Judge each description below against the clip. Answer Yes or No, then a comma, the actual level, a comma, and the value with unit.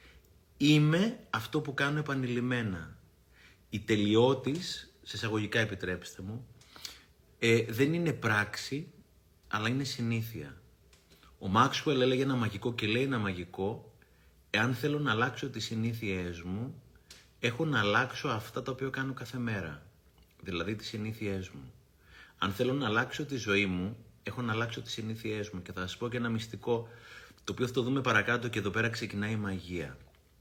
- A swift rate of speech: No, average, 155 wpm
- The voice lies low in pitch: Yes, low, 115 Hz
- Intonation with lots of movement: No, average, 4.5 semitones